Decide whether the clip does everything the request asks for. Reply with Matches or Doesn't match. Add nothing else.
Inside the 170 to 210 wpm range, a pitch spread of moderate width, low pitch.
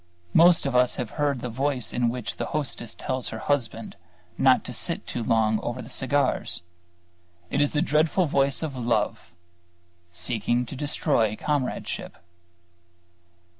Doesn't match